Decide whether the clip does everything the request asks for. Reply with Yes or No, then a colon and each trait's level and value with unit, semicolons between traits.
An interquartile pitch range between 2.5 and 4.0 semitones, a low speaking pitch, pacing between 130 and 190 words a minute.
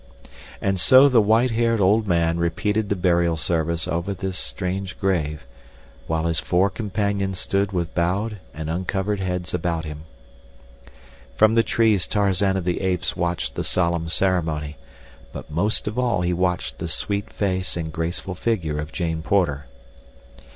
Yes: average, 3.2 semitones; very low, 90 Hz; average, 160 wpm